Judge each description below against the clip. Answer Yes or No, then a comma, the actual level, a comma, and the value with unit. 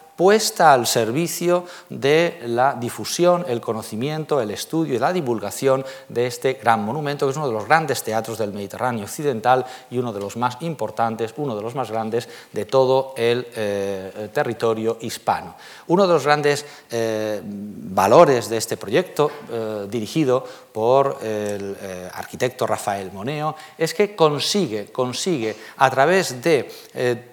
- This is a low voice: Yes, low, 125 Hz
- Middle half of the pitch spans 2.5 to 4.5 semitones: No, average, 4.9 semitones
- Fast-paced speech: No, average, 150 wpm